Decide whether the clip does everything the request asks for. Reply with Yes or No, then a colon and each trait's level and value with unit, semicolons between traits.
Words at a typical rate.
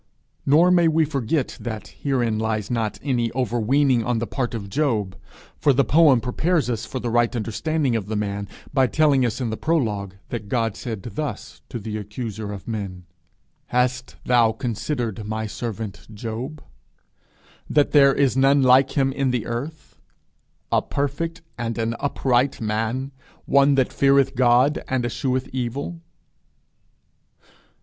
Yes: average, 150 wpm